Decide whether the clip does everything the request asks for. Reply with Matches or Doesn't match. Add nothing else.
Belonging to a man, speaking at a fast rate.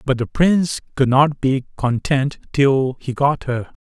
Doesn't match